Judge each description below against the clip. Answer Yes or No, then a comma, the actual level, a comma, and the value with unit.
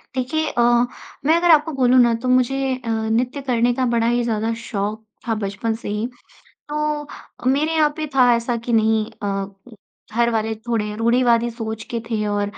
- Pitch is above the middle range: Yes, high, 235 Hz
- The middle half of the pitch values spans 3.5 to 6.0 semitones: No, narrow, 2.5 semitones